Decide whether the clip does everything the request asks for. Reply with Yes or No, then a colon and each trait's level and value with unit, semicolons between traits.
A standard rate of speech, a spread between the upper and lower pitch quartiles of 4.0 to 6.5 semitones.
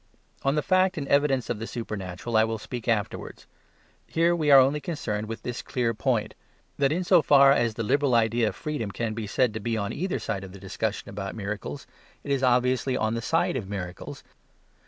No: fast, 210 wpm; average, 4.5 semitones